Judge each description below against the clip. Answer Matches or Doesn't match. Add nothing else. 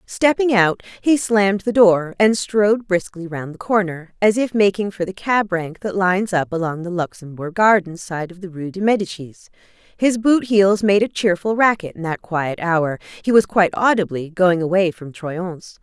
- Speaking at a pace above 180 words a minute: Matches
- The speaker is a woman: Matches